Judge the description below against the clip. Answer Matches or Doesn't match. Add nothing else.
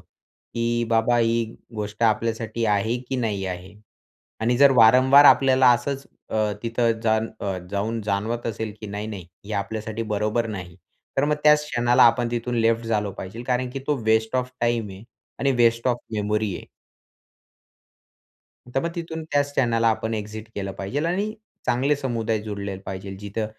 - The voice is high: Doesn't match